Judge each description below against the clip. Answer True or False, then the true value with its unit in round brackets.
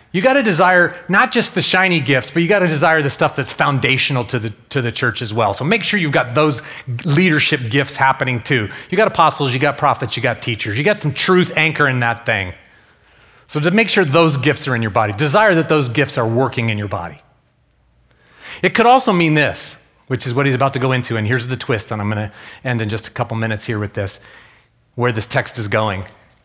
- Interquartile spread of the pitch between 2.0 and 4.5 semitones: False (5.1 semitones)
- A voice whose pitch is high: False (135 Hz)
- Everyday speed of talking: False (230 wpm)